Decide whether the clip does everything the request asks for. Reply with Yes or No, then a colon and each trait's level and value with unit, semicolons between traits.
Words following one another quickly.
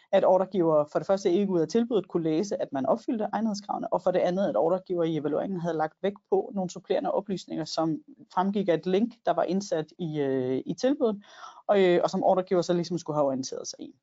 Yes: fast, 230 wpm